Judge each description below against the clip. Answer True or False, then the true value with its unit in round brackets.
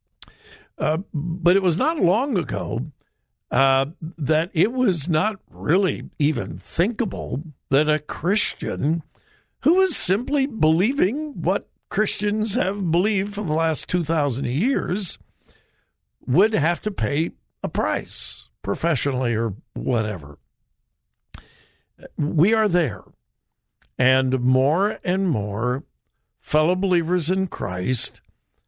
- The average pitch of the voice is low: False (160 Hz)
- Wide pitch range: True (6.1 semitones)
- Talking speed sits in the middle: False (105 wpm)